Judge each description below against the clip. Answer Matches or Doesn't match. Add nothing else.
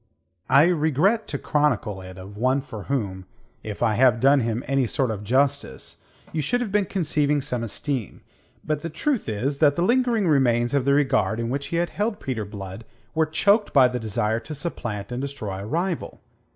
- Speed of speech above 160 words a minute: Matches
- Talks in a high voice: Doesn't match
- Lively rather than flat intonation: Matches